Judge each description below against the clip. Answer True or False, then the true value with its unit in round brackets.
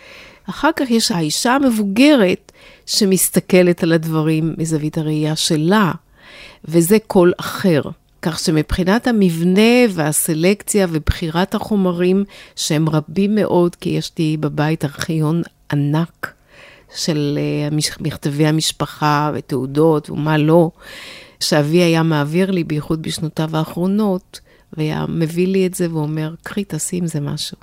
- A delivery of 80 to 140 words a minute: True (115 wpm)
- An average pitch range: True (3.5 semitones)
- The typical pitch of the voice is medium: True (165 Hz)